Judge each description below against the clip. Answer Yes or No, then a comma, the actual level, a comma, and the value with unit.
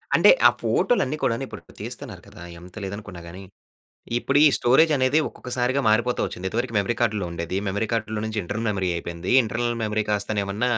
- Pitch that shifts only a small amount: No, average, 3.9 semitones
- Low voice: Yes, low, 110 Hz